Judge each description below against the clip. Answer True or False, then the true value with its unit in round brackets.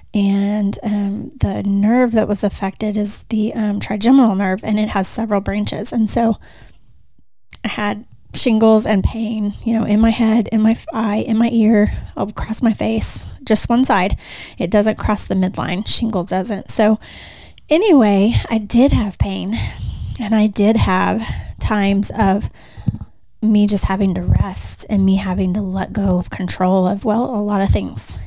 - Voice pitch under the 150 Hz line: False (210 Hz)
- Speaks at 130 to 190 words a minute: True (170 wpm)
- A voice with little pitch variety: True (2.1 semitones)